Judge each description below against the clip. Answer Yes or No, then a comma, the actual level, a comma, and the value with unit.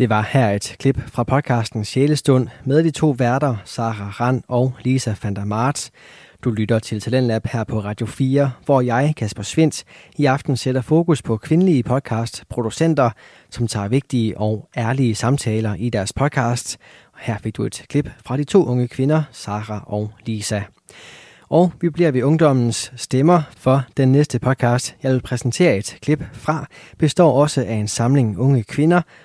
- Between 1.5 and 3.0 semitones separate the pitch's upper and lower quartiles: No, average, 4.1 semitones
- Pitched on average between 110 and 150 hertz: Yes, low, 125 Hz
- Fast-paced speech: No, average, 165 wpm